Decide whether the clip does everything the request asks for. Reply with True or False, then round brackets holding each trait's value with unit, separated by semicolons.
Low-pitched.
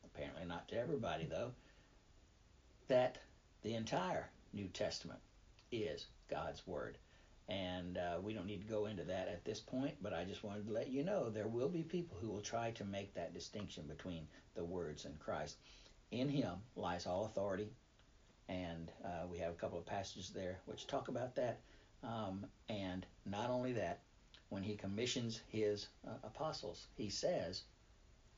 True (105 Hz)